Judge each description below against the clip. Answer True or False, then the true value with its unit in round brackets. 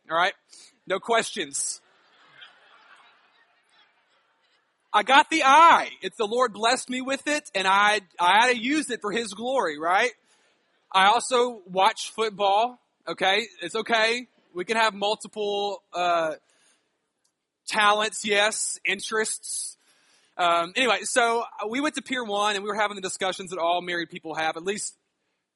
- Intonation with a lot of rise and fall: False (3.7 semitones)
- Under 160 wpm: True (145 wpm)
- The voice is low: False (210 Hz)